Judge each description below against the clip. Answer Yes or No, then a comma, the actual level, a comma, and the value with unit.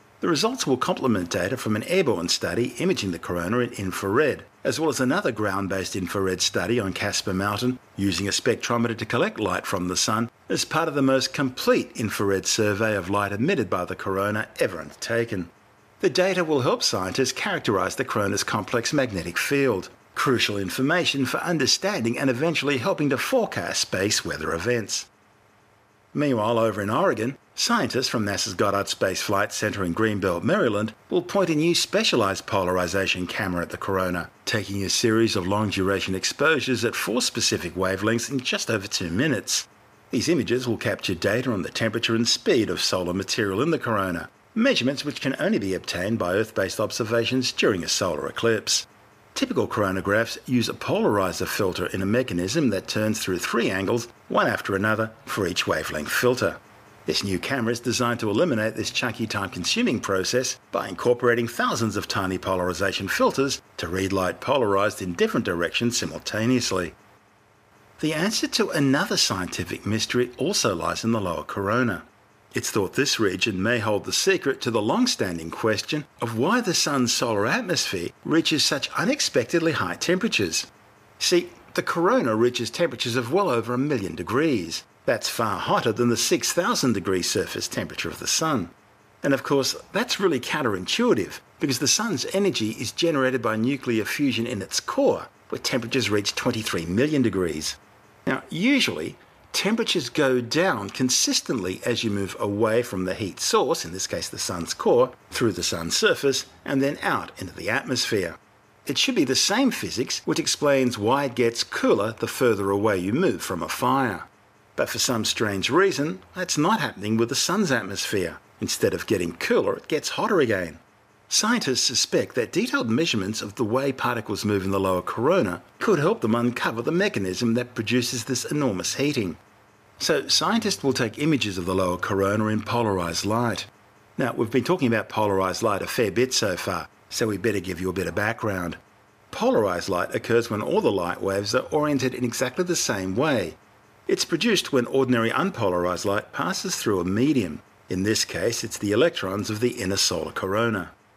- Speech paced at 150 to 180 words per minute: Yes, average, 175 wpm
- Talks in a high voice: No, low, 115 Hz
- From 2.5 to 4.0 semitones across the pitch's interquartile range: No, average, 4.7 semitones